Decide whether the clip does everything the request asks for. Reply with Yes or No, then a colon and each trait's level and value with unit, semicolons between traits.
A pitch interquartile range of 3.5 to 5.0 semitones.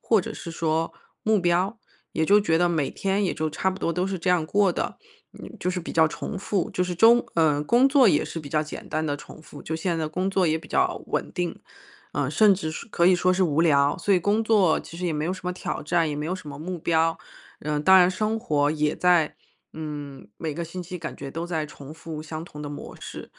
No: average, 3.1 semitones